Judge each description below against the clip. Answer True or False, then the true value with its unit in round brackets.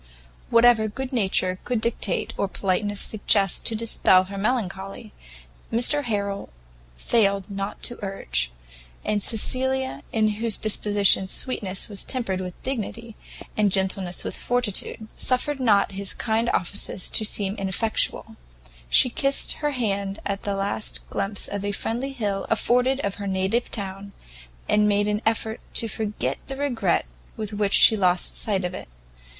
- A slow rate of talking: False (145 wpm)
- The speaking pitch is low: False (210 Hz)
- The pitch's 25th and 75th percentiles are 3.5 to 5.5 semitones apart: False (2.9 semitones)